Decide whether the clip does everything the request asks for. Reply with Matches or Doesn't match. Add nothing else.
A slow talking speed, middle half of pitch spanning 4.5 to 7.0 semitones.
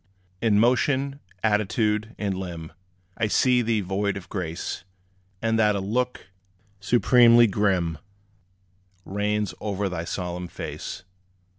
Doesn't match